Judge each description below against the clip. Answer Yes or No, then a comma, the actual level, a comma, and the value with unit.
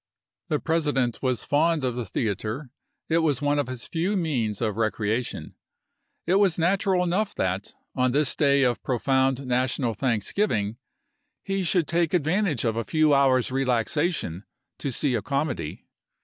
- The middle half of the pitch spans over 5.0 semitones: Yes, wide, 5.4 semitones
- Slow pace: No, average, 155 wpm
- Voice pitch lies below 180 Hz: Yes, low, 135 Hz